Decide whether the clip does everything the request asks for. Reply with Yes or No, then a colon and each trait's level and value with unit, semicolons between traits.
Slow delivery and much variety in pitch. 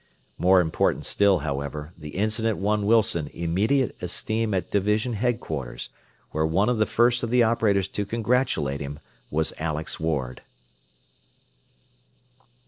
Yes: slow, 130 wpm; wide, 6.1 semitones